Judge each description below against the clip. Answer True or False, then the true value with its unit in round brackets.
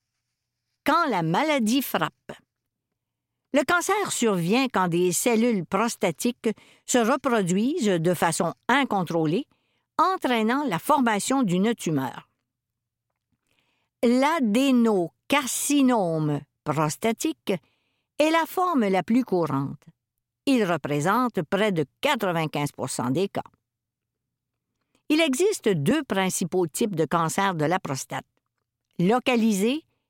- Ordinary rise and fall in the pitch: False (7.8 semitones)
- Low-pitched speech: False (205 Hz)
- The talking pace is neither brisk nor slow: False (95 wpm)